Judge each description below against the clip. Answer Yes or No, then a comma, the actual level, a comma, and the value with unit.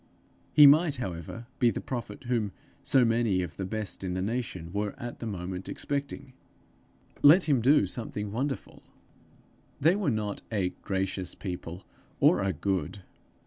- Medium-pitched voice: No, low, 110 Hz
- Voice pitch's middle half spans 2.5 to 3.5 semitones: No, wide, 5.4 semitones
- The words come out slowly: No, average, 150 wpm